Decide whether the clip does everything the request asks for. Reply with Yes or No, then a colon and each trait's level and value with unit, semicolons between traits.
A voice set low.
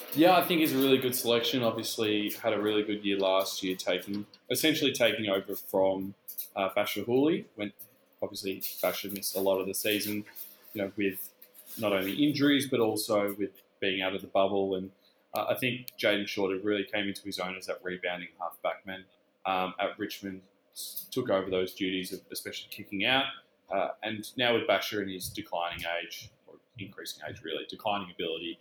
Yes: low, 100 Hz